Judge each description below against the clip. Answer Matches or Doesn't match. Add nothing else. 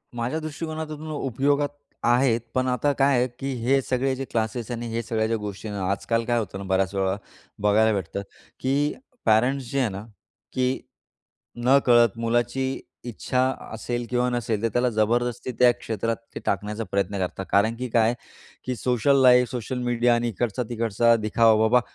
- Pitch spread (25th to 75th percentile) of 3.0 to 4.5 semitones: Doesn't match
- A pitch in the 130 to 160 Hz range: Doesn't match